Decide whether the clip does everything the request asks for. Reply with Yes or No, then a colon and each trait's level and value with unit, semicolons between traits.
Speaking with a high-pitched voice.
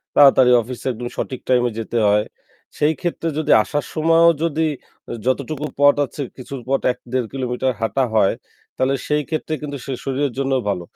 No: low, 135 Hz